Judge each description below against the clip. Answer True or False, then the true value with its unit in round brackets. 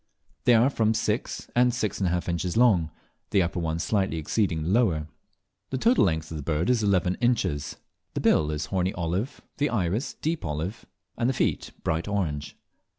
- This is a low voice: True (95 Hz)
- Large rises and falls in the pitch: True (6.0 semitones)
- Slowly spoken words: False (190 wpm)